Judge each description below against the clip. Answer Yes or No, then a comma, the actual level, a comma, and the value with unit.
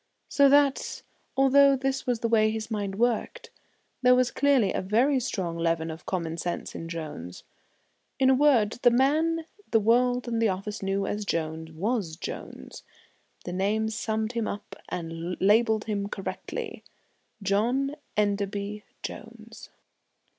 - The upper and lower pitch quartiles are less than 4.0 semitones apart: No, average, 4.5 semitones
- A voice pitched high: Yes, high, 215 Hz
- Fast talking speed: No, average, 145 wpm